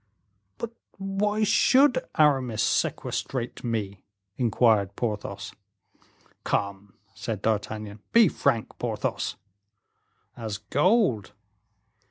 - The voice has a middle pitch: No, low, 115 Hz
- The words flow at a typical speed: No, slow, 80 wpm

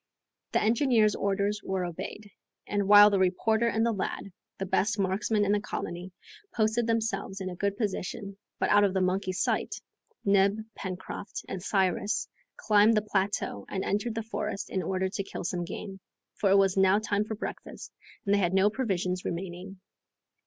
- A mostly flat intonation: Yes, narrow, 1.9 semitones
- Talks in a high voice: Yes, high, 200 Hz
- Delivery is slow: No, average, 175 wpm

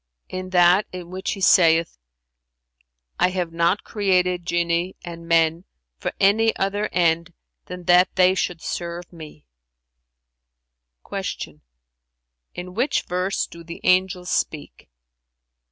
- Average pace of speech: No, slow, 120 wpm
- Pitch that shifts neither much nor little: No, narrow, 2.3 semitones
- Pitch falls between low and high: Yes, medium, 175 Hz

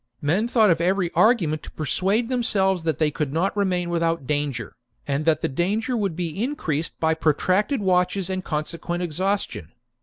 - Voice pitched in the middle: Yes, medium, 175 Hz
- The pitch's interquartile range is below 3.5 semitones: No, average, 4.2 semitones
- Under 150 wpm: No, average, 170 wpm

